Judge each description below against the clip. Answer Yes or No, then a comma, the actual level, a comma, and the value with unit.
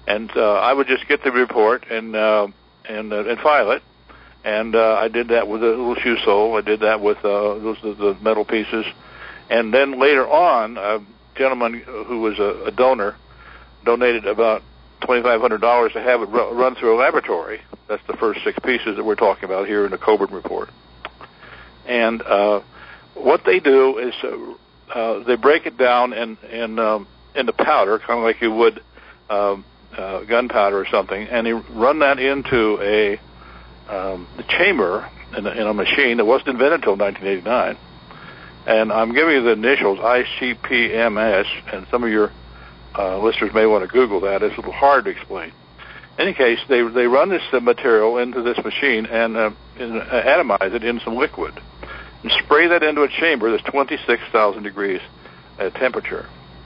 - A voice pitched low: Yes, low, 115 Hz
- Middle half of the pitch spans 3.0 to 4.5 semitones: Yes, average, 4.1 semitones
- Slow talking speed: No, average, 185 wpm